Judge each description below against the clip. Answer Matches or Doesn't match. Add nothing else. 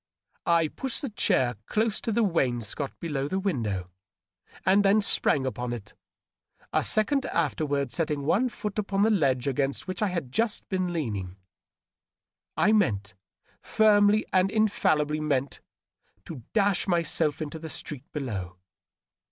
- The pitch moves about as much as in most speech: Doesn't match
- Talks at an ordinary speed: Matches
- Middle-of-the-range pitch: Matches